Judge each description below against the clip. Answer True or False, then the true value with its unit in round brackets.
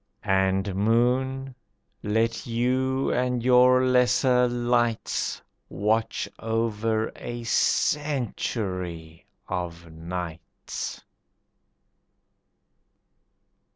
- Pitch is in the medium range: False (115 Hz)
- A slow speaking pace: True (60 wpm)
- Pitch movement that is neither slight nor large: True (4.6 semitones)